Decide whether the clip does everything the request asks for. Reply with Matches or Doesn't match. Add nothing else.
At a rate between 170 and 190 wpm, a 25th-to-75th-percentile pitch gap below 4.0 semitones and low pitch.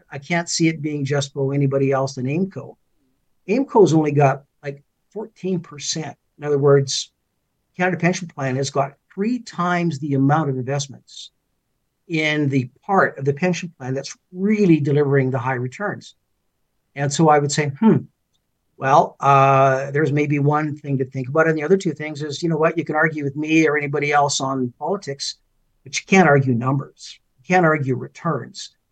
Doesn't match